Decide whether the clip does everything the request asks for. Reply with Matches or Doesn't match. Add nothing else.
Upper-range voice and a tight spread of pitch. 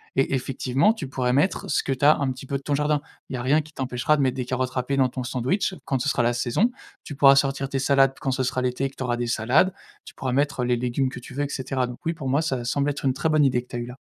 Doesn't match